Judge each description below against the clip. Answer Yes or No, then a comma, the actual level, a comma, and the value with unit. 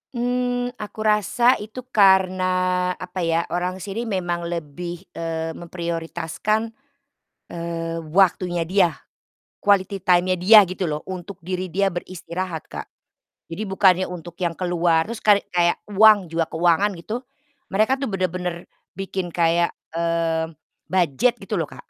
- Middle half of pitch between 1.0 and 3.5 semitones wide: Yes, average, 2.8 semitones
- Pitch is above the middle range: No, medium, 180 Hz